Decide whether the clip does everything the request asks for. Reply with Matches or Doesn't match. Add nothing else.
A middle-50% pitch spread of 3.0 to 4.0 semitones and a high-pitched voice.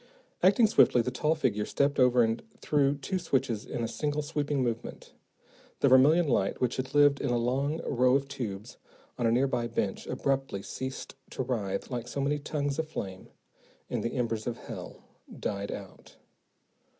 Doesn't match